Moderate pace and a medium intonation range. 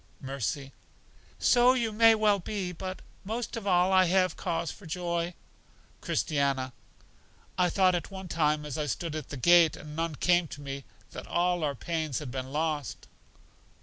Yes: average, 170 wpm; average, 4.0 semitones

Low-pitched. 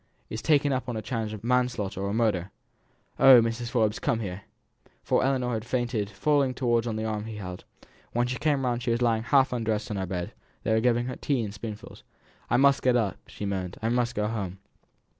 Yes: low, 115 Hz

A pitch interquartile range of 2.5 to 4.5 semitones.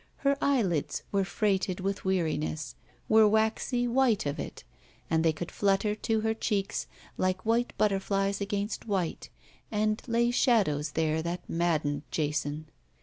No: average, 5.1 semitones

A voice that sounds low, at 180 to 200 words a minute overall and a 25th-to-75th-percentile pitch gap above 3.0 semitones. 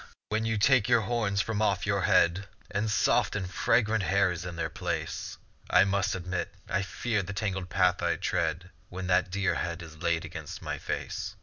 No: very low, 95 Hz; average, 195 wpm; average, 2.7 semitones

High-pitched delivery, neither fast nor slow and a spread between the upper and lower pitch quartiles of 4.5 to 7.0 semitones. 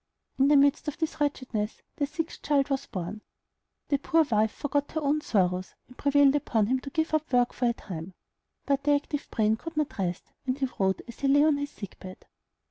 No: very high, 275 Hz; fast, 215 wpm; average, 5.1 semitones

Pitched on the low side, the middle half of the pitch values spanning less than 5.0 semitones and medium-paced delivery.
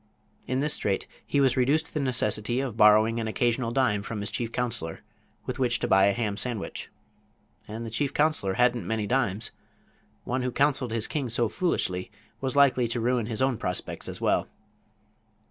Yes: low, 120 Hz; average, 3.5 semitones; average, 185 wpm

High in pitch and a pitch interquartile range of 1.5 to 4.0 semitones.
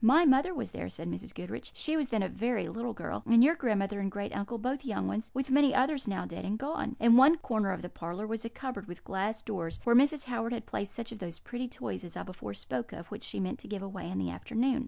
No: high, 225 Hz; average, 5.1 semitones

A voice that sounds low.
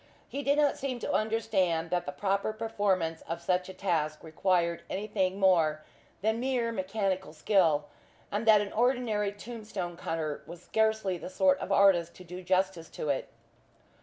No: high, 190 Hz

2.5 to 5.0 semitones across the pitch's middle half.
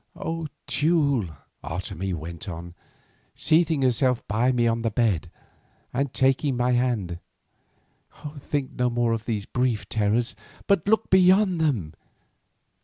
No: wide, 5.5 semitones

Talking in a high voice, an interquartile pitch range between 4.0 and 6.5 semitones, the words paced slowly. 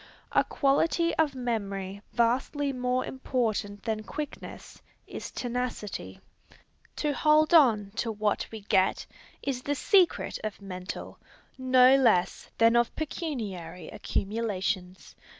Yes: high, 235 Hz; average, 5.1 semitones; slow, 115 wpm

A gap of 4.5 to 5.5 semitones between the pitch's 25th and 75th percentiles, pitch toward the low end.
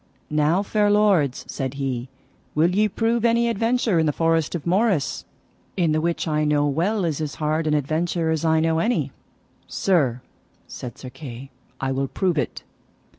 No: average, 4.8 semitones; medium, 160 Hz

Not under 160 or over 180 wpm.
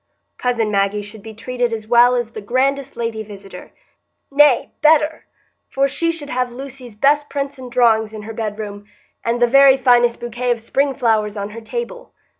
Yes: average, 175 wpm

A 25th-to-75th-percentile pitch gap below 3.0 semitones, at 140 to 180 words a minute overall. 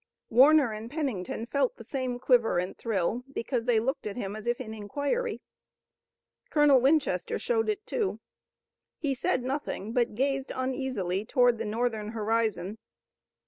No: average, 3.8 semitones; average, 145 wpm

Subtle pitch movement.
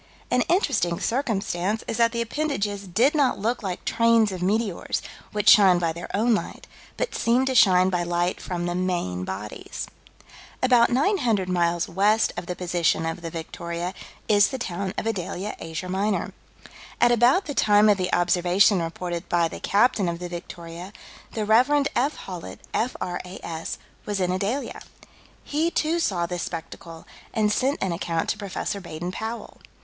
No: average, 4.9 semitones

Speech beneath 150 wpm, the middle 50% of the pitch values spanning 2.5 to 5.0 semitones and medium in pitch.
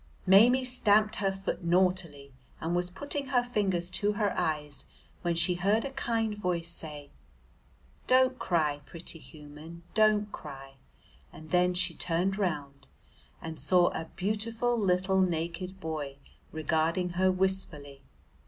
Yes: slow, 135 wpm; average, 4.3 semitones; medium, 180 Hz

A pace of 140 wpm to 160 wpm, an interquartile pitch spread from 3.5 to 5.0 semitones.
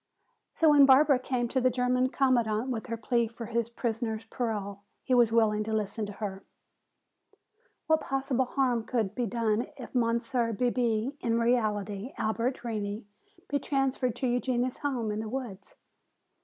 No: average, 155 wpm; average, 2.7 semitones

